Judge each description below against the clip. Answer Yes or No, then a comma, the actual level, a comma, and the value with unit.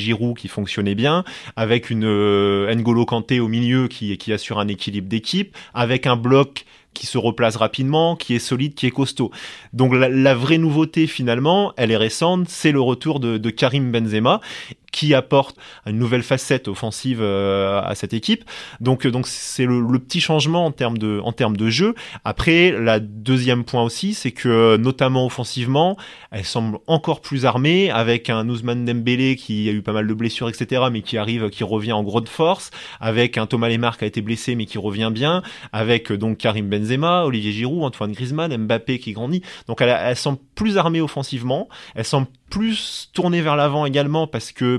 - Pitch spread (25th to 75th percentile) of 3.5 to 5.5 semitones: Yes, average, 3.9 semitones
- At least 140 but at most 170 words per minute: No, average, 190 wpm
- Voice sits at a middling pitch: No, low, 120 Hz